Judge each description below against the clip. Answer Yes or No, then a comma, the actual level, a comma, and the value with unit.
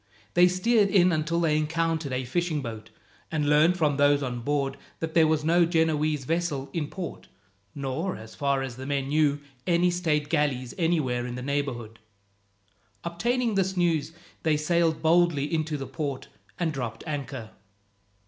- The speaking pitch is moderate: Yes, medium, 155 Hz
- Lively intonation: No, average, 3.6 semitones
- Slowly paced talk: No, average, 160 wpm